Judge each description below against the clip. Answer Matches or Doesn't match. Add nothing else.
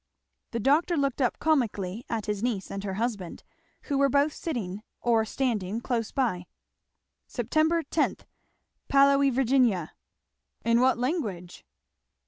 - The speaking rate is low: Matches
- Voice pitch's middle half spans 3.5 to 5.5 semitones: Matches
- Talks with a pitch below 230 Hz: Doesn't match